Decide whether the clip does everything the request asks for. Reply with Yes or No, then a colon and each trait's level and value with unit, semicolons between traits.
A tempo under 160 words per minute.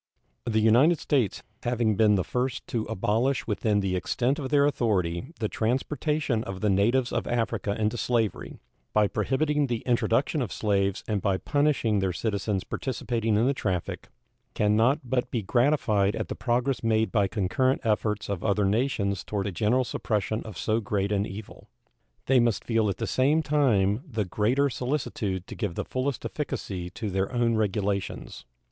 No: average, 170 wpm